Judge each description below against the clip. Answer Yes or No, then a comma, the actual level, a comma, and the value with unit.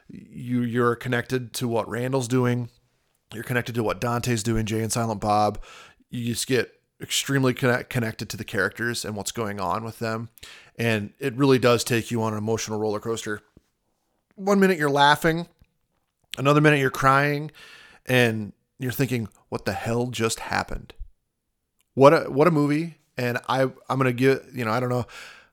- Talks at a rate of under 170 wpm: No, average, 175 wpm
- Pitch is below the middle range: Yes, low, 120 Hz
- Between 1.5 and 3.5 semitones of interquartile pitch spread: Yes, average, 2.8 semitones